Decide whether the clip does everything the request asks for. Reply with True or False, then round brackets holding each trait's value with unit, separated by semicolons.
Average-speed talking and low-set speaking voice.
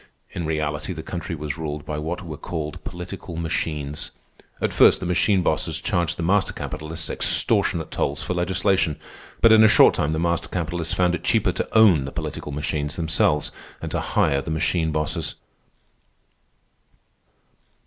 True (160 wpm; 80 Hz)